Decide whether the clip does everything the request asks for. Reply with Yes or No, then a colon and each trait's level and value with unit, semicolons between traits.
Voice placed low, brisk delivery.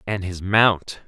No: very low, 95 Hz; average, 170 wpm